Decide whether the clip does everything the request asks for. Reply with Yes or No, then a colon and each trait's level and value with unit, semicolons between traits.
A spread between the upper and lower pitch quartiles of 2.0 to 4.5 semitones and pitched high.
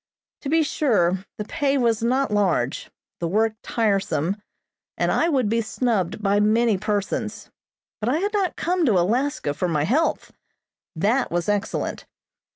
No: wide, 5.6 semitones; high, 215 Hz